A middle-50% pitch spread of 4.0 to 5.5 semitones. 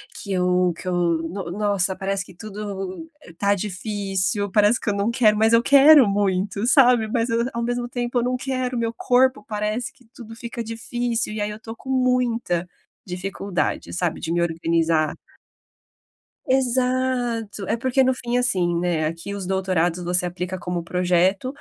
Yes: average, 5.0 semitones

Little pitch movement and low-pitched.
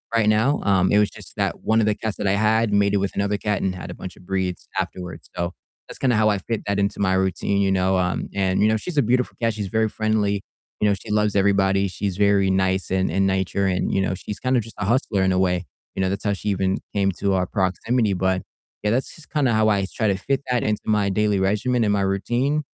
Yes: narrow, 2.2 semitones; low, 100 Hz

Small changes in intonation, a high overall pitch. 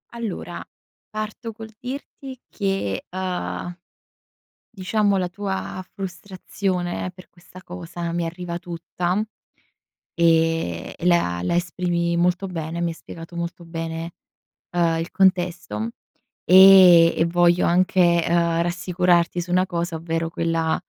No: narrow, 1.8 semitones; medium, 175 Hz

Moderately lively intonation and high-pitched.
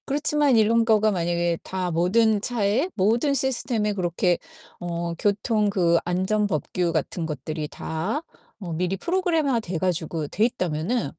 Yes: average, 5.0 semitones; high, 195 Hz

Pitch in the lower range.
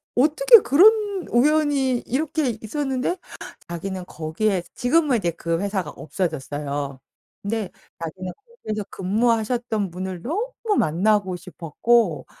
No: high, 215 Hz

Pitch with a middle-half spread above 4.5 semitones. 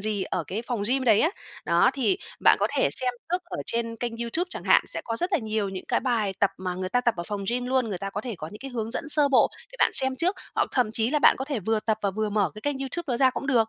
No: average, 4.0 semitones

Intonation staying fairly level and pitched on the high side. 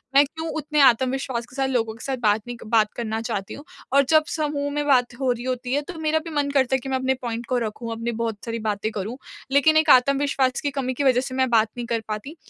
No: average, 3.3 semitones; very high, 255 Hz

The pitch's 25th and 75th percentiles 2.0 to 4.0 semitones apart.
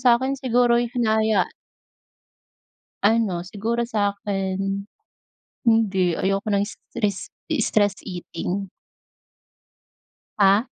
Yes: average, 2.9 semitones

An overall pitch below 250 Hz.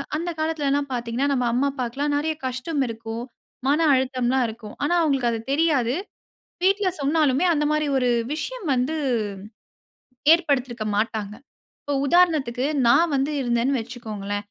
No: very high, 270 Hz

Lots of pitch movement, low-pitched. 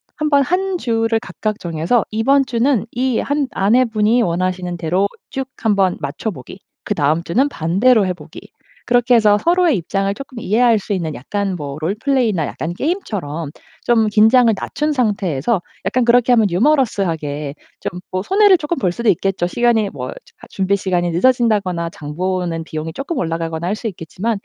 No: wide, 5.8 semitones; high, 205 Hz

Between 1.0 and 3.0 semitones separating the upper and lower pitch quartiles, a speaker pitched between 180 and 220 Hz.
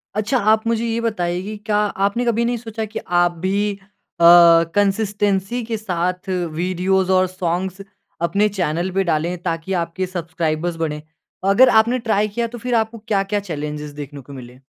No: average, 4.2 semitones; high, 190 Hz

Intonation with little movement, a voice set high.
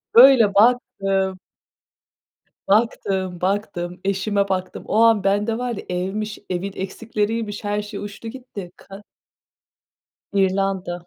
Yes: narrow, 2.3 semitones; high, 200 Hz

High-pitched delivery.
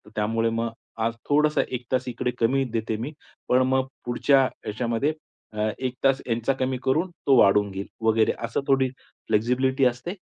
No: low, 125 Hz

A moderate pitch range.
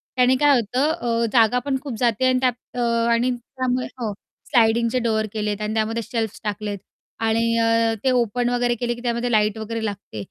No: narrow, 2.1 semitones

